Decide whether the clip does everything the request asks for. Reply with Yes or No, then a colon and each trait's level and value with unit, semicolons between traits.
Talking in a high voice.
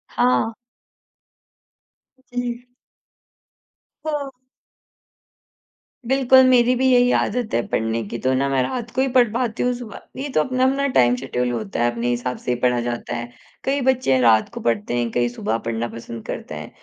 No: low, 135 Hz